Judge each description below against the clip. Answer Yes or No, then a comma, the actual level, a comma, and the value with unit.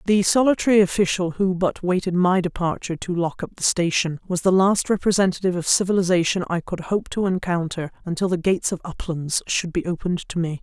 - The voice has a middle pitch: Yes, medium, 180 Hz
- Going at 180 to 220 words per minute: Yes, average, 190 wpm